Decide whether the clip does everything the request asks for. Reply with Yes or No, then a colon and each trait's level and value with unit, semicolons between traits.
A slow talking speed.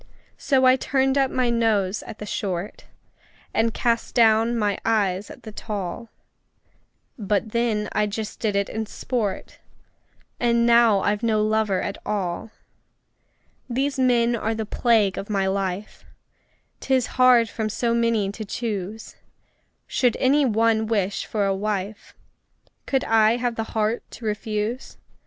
No: average, 145 wpm